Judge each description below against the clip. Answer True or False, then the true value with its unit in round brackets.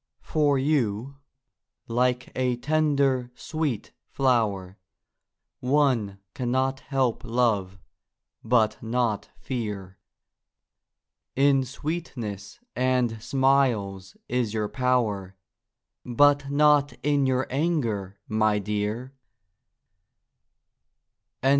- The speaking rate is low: True (80 wpm)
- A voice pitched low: True (125 Hz)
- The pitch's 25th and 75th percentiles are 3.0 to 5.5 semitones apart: True (4.4 semitones)